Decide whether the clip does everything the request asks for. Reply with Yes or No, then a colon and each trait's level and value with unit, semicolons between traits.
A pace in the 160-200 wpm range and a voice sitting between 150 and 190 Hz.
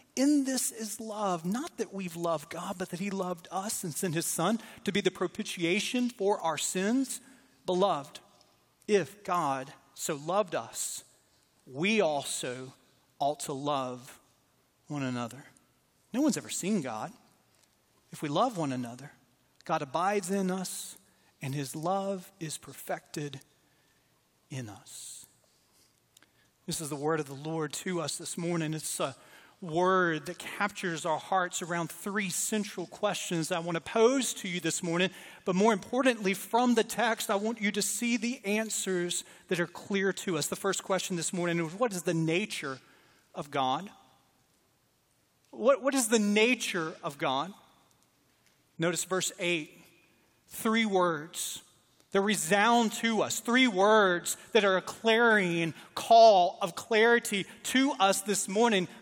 No: average, 150 wpm; medium, 185 Hz